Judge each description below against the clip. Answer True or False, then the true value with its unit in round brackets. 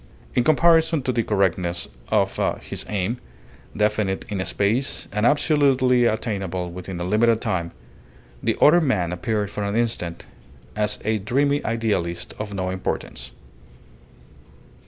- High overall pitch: False (105 Hz)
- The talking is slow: True (130 wpm)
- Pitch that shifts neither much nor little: True (4.8 semitones)